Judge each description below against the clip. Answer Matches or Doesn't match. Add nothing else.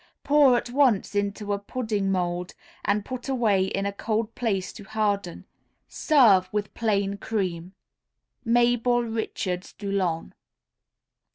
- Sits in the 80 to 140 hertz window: Doesn't match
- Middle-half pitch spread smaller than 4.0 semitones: Matches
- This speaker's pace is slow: Matches